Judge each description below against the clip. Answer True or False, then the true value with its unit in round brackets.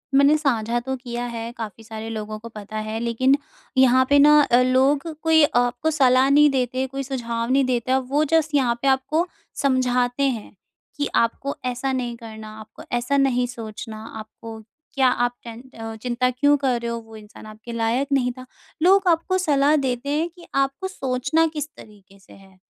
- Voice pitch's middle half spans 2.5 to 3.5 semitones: True (3.2 semitones)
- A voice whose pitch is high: True (250 Hz)